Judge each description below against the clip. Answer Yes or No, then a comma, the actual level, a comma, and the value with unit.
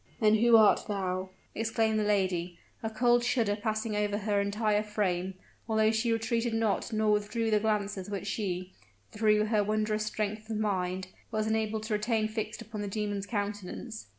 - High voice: Yes, high, 215 Hz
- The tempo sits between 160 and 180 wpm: Yes, average, 170 wpm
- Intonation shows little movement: Yes, narrow, 1.4 semitones